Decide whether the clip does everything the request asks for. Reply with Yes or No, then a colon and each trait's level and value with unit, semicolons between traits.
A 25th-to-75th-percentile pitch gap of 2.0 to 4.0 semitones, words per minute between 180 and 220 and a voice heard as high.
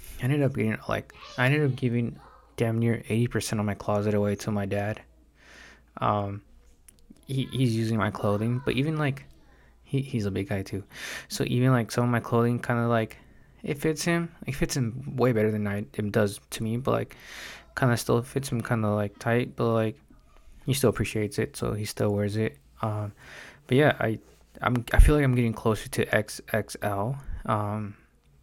No: average, 3.2 semitones; average, 200 wpm; low, 115 Hz